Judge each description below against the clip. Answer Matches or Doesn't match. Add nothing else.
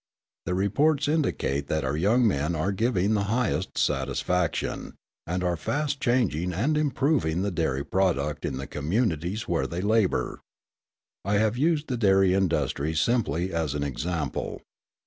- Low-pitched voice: Matches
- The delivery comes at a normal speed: Matches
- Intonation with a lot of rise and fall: Matches